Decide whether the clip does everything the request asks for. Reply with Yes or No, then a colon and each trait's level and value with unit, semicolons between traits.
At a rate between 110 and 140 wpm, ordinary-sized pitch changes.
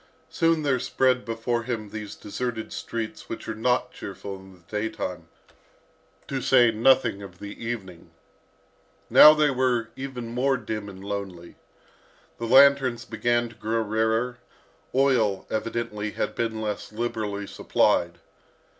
Yes: slow, 135 wpm; average, 3.3 semitones